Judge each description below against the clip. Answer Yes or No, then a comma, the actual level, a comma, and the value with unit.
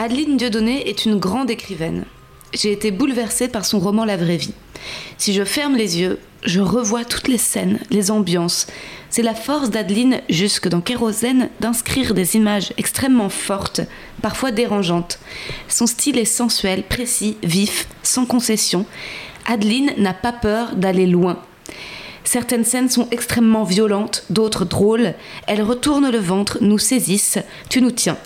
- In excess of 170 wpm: No, average, 150 wpm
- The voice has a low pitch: No, high, 220 Hz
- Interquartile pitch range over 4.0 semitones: No, average, 3.5 semitones